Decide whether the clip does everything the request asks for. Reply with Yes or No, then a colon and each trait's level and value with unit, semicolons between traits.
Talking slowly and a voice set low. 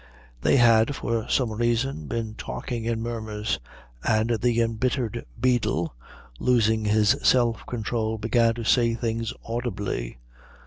Yes: slow, 125 wpm; low, 115 Hz